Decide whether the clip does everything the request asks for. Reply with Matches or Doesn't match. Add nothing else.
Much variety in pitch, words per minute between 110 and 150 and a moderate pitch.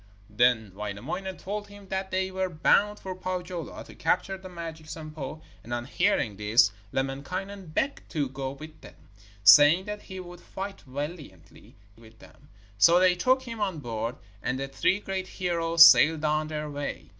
Doesn't match